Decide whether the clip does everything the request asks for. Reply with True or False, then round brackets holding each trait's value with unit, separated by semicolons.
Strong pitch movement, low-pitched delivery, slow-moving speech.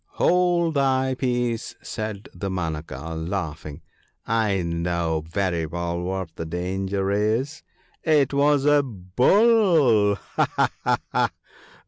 True (7.6 semitones; 100 Hz; 105 wpm)